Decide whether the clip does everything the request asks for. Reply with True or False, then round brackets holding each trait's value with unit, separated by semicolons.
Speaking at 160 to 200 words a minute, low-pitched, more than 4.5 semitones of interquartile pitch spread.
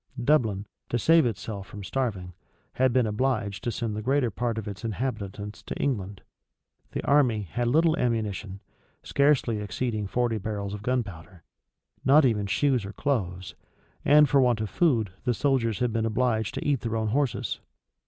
False (165 wpm; 115 Hz; 4.0 semitones)